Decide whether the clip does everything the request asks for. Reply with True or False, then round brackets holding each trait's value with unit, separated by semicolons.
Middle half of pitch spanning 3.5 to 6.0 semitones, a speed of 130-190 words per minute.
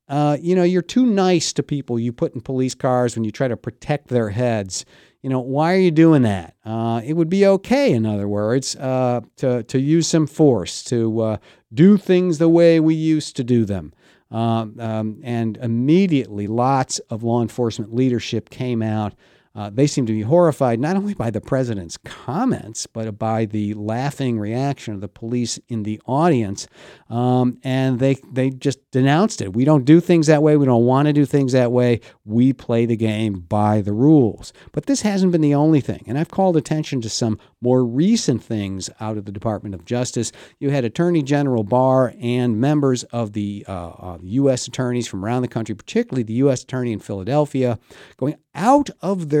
False (4.7 semitones; 200 wpm)